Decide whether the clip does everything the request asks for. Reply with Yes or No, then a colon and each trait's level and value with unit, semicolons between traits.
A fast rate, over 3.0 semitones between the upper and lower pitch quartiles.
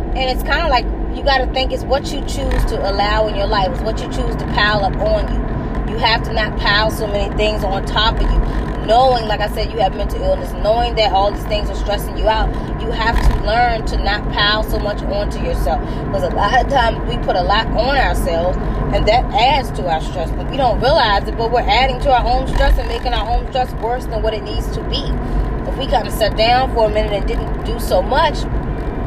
Yes: fast, 250 wpm; average, 3.6 semitones